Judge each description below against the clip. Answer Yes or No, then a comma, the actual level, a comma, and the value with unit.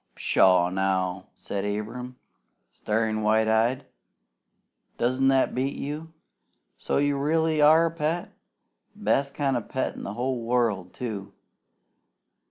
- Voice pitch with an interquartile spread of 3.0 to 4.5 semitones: No, average, 4.9 semitones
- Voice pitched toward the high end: No, low, 125 Hz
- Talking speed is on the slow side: Yes, slow, 130 wpm